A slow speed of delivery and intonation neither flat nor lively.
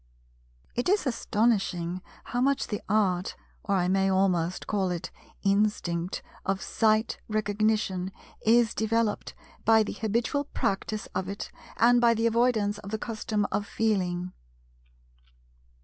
Yes: slow, 120 wpm; average, 3.0 semitones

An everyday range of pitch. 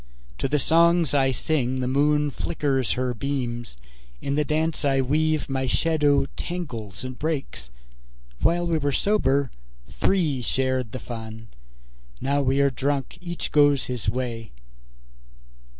Yes: average, 3.1 semitones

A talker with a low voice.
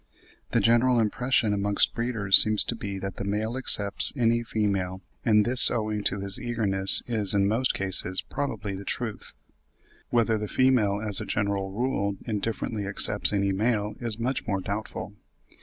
Yes: low, 105 Hz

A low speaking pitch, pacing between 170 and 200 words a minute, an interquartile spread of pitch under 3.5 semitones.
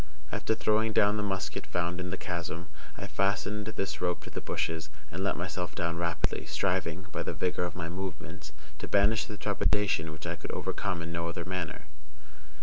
Yes: very low, 90 Hz; average, 190 wpm; average, 2.9 semitones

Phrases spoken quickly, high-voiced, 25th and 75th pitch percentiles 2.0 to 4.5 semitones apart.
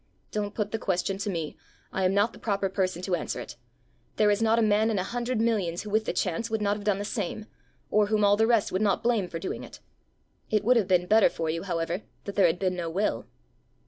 Yes: fast, 255 wpm; high, 205 Hz; average, 2.8 semitones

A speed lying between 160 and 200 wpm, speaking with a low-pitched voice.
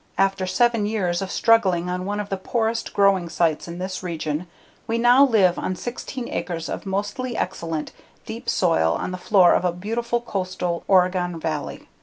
No: average, 175 wpm; medium, 185 Hz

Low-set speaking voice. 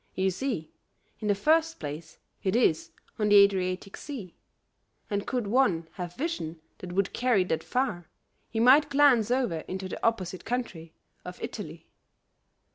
No: high, 200 Hz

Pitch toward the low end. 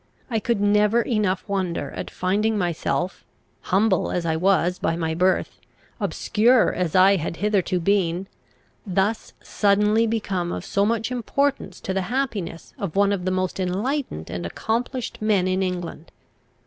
No: high, 195 Hz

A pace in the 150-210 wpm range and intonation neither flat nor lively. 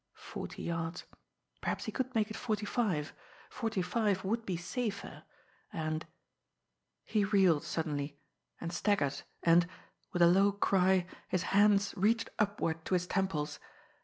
No: slow, 135 wpm; average, 3.9 semitones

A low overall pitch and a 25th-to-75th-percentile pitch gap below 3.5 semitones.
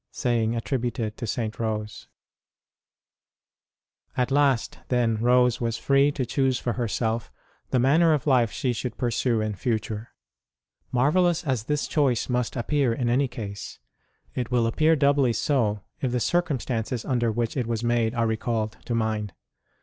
Yes: low, 120 Hz; average, 2.8 semitones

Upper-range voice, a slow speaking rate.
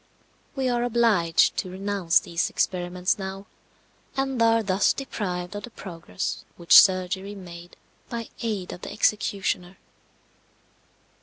Yes: high, 195 Hz; slow, 125 wpm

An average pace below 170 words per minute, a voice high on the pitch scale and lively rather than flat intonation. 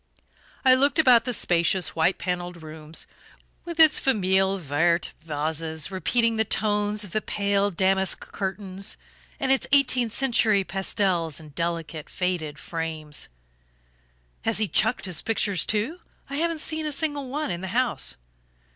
Yes: average, 145 wpm; high, 195 Hz; wide, 6.2 semitones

